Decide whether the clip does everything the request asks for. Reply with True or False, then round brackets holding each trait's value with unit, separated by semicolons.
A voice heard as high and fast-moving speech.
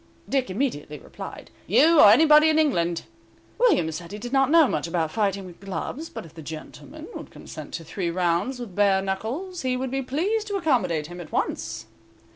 False (205 Hz; 195 wpm)